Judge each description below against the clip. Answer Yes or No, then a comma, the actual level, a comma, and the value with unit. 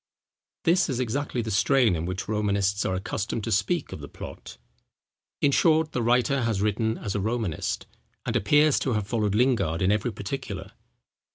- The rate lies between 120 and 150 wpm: No, average, 175 wpm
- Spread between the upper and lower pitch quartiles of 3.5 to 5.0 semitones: Yes, average, 4.7 semitones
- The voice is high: No, low, 110 Hz